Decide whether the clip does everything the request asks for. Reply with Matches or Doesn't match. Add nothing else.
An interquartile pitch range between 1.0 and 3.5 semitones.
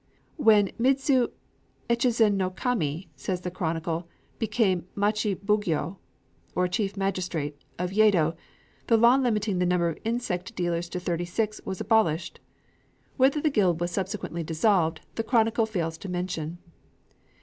Doesn't match